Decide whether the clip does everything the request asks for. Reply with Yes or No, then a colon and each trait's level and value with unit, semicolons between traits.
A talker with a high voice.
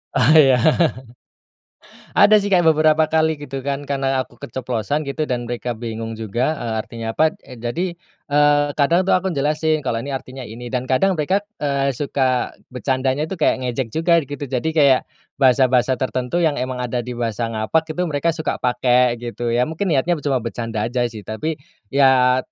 No: low, 135 Hz